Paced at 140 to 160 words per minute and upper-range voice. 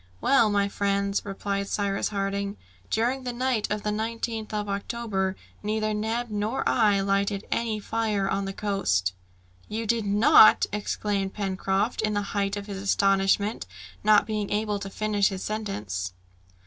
Yes: average, 150 wpm; high, 205 Hz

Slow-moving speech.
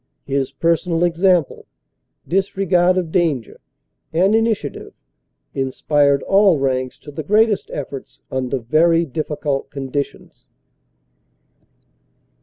Yes: slow, 90 wpm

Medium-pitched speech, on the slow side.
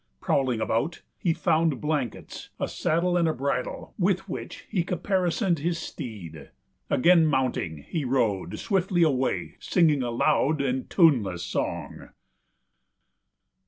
Yes: medium, 150 Hz; slow, 120 wpm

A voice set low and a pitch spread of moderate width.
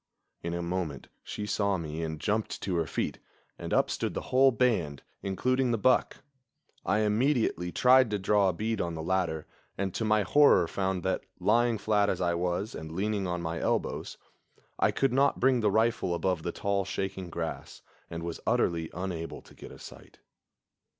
Yes: very low, 95 Hz; average, 4.3 semitones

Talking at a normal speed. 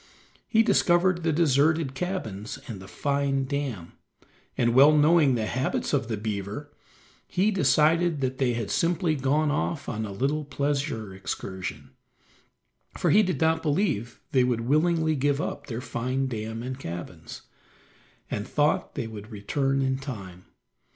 Yes: average, 150 wpm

